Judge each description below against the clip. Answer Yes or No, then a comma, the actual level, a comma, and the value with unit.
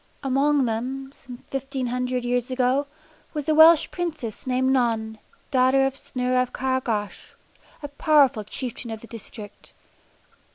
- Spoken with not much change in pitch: Yes, narrow, 2.0 semitones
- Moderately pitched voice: No, very high, 255 Hz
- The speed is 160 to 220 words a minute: No, average, 140 wpm